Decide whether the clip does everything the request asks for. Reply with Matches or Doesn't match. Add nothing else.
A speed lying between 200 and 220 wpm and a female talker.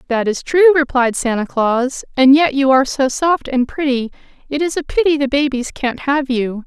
Matches